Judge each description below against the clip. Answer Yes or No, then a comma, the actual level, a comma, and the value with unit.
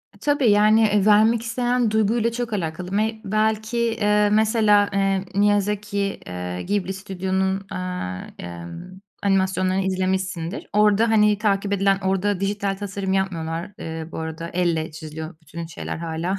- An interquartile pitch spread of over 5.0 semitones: No, narrow, 2.6 semitones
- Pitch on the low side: No, high, 195 Hz